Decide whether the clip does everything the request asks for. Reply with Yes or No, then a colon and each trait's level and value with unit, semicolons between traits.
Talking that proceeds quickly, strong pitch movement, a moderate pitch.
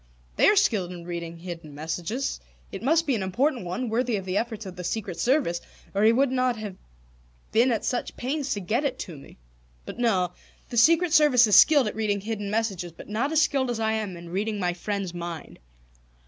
No: fast, 215 wpm; wide, 5.9 semitones; high, 215 Hz